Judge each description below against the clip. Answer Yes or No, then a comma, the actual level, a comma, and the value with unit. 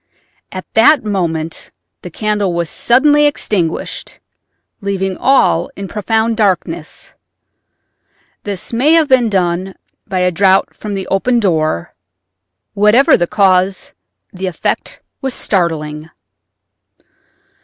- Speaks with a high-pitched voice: Yes, high, 195 Hz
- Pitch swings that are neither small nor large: Yes, average, 4.0 semitones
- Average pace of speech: No, slow, 110 wpm